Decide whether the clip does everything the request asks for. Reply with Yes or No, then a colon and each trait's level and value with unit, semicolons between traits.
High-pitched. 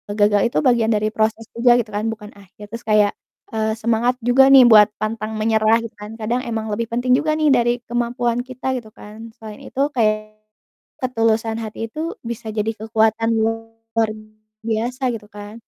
Yes: high, 225 Hz